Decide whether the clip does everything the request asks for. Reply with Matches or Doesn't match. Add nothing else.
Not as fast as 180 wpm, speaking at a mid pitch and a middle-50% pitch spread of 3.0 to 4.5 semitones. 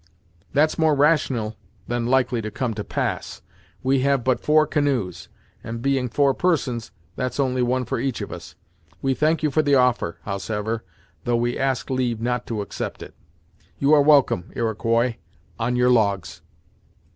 Doesn't match